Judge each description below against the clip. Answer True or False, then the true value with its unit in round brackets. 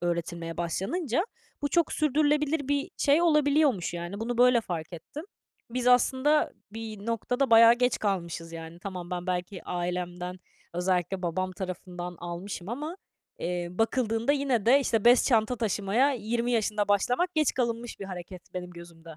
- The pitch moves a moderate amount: False (6.1 semitones)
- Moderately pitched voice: False (215 Hz)